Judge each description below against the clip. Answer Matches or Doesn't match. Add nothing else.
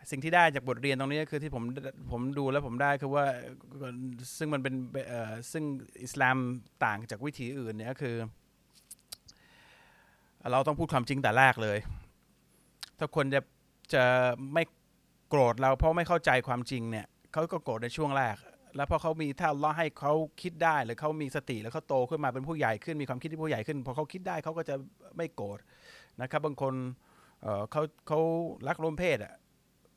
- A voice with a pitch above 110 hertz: Matches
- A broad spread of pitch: Doesn't match